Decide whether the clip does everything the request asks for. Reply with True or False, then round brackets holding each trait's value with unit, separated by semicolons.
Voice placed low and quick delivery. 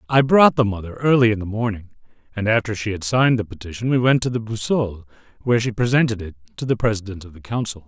True (110 Hz; 230 wpm)